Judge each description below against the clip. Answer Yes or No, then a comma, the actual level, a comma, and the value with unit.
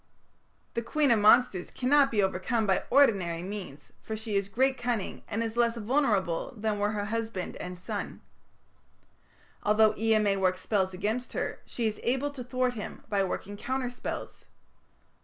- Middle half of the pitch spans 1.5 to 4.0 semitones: Yes, average, 3.7 semitones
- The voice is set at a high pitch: Yes, high, 220 Hz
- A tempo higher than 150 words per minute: Yes, average, 165 wpm